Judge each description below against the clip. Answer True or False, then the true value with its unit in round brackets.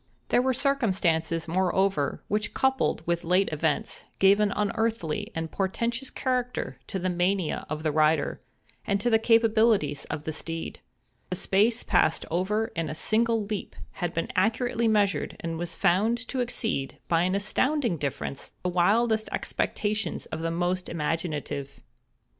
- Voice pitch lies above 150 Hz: True (190 Hz)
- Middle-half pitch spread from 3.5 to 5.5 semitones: True (5.2 semitones)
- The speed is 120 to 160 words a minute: True (150 wpm)